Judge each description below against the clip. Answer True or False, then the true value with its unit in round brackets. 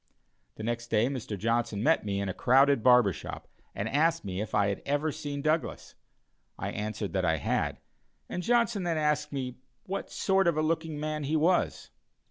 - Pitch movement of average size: False (6.6 semitones)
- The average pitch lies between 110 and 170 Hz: True (140 Hz)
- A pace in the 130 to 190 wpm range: True (185 wpm)